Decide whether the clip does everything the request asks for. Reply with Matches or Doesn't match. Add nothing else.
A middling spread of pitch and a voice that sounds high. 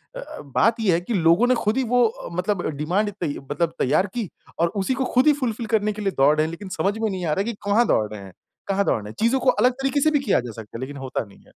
Doesn't match